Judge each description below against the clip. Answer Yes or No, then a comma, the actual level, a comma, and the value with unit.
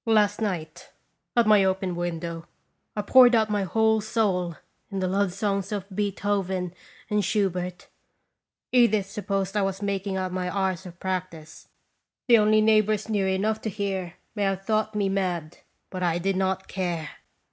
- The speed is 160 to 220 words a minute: Yes, average, 165 wpm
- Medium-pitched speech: No, high, 195 Hz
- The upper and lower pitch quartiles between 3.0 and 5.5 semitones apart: No, narrow, 2.5 semitones